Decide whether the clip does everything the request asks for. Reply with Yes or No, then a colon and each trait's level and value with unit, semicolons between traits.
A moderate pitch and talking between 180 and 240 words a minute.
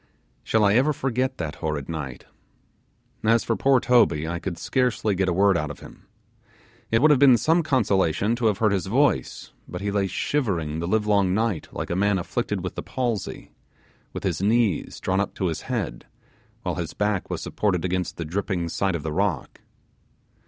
No: low, 100 Hz; average, 195 wpm